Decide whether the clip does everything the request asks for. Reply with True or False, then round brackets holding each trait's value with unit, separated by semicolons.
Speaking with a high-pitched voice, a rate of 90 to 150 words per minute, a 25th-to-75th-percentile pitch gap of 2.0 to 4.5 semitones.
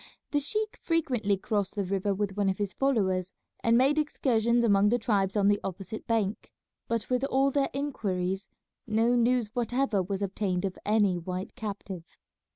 False (210 Hz; 165 wpm; 4.0 semitones)